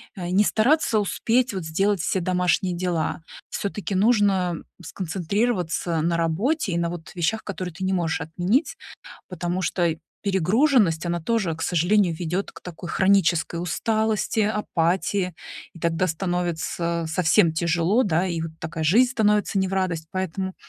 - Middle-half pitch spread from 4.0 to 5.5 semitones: No, average, 3.3 semitones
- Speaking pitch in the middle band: Yes, medium, 180 Hz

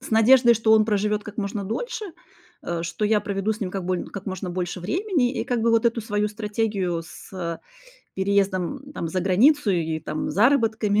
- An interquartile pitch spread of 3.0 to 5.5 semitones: Yes, average, 3.5 semitones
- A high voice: Yes, high, 210 Hz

